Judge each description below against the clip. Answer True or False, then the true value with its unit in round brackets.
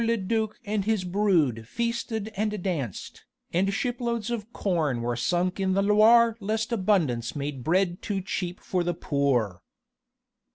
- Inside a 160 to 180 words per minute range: False (150 wpm)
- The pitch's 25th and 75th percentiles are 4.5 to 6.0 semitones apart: True (5.5 semitones)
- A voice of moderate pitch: False (195 Hz)